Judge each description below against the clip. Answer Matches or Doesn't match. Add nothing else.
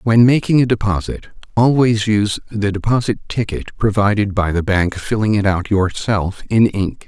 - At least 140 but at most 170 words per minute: Matches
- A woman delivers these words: Doesn't match